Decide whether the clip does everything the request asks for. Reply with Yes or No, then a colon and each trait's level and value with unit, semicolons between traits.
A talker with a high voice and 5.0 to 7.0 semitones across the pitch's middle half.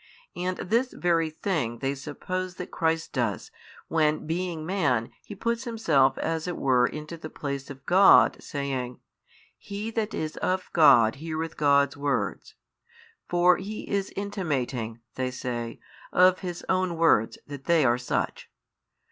No: medium, 160 Hz; average, 5.3 semitones